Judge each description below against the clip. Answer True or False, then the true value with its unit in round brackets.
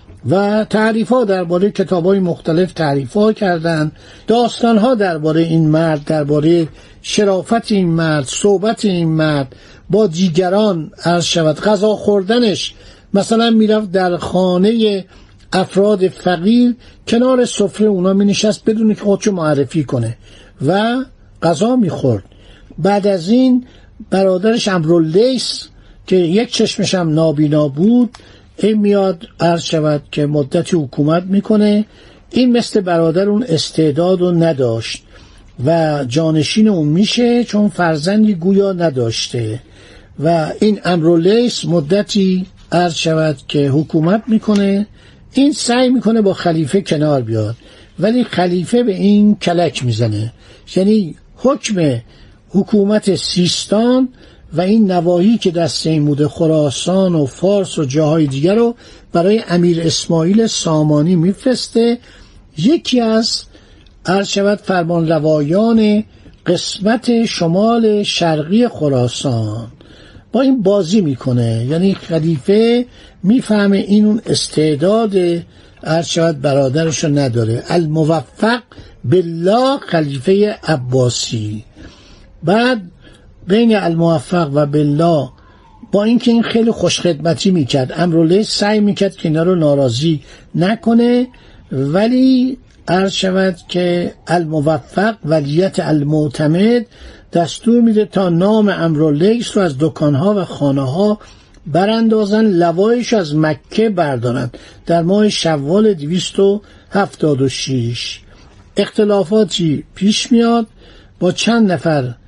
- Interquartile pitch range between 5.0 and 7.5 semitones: True (5.5 semitones)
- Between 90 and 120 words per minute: True (110 wpm)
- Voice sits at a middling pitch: True (180 Hz)